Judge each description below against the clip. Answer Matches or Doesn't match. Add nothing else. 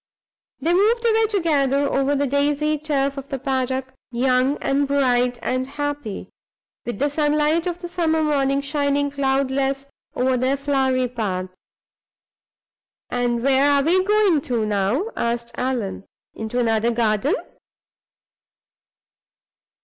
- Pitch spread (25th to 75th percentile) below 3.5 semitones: Matches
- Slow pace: Matches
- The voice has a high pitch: Matches